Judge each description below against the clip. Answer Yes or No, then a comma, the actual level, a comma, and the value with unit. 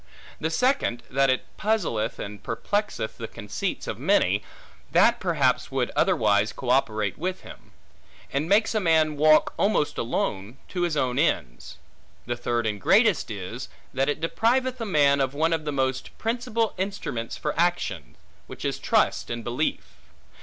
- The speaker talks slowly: No, average, 160 wpm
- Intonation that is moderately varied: No, wide, 7.9 semitones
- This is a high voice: No, medium, 145 Hz